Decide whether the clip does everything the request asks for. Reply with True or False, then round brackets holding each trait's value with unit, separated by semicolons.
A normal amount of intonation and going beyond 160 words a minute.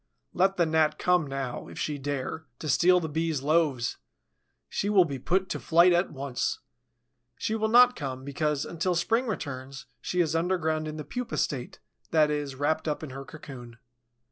True (4.2 semitones; 180 wpm)